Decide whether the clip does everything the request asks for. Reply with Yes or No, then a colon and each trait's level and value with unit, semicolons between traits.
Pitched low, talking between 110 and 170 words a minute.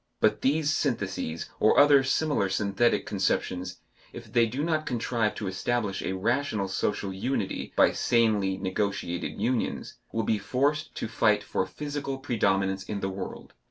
Yes: low, 110 Hz; average, 150 wpm